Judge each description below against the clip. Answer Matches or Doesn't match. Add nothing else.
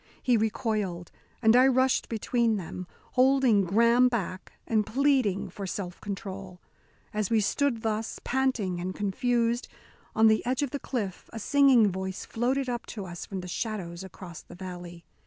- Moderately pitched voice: Doesn't match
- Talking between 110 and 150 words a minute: Doesn't match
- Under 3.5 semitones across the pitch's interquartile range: Doesn't match